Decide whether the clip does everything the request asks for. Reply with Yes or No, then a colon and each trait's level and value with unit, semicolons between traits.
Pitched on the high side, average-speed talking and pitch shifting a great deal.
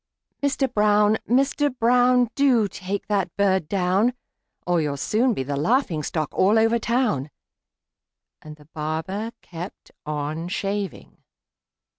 No: high, 200 Hz; slow, 125 wpm; wide, 6.6 semitones